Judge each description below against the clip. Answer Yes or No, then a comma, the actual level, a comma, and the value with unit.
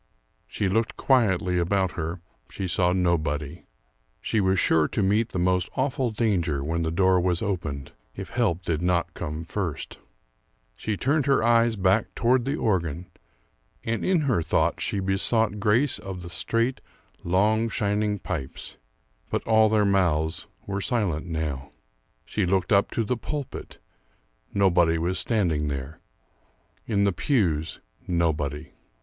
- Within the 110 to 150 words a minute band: Yes, average, 145 wpm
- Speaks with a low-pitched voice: Yes, very low, 95 Hz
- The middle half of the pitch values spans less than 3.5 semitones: No, average, 4.7 semitones